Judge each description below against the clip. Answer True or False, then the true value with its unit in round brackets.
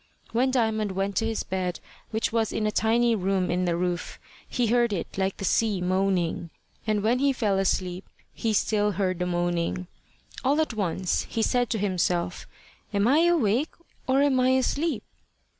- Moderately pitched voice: False (210 Hz)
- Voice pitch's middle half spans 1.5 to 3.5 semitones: False (4.4 semitones)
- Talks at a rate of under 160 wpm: False (175 wpm)